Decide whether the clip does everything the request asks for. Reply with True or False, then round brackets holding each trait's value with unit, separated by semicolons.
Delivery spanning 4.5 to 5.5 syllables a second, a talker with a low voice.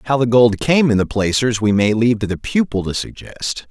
True (5.1 syllables/s; 115 Hz)